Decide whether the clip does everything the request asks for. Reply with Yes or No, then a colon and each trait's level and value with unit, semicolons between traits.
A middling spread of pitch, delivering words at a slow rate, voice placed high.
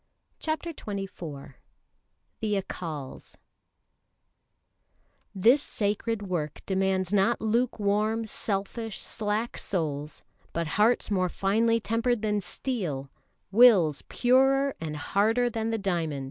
Yes: average, 3.9 semitones; slow, 100 wpm; high, 205 Hz